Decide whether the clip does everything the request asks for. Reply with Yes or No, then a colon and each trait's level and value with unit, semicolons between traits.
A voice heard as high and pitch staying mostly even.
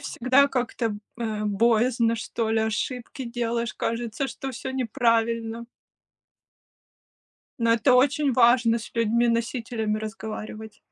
Yes: high, 230 Hz; narrow, 1.9 semitones